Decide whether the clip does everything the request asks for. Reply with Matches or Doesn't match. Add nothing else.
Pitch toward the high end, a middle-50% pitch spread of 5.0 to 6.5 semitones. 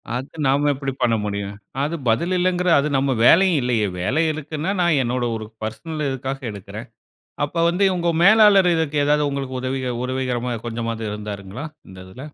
Doesn't match